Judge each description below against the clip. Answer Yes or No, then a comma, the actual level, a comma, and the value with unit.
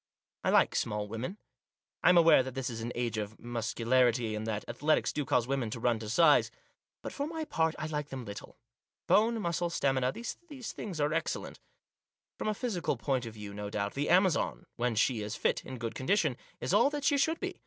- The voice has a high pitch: No, low, 130 Hz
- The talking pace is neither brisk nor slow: No, fast, 215 wpm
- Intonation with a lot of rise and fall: Yes, wide, 7.0 semitones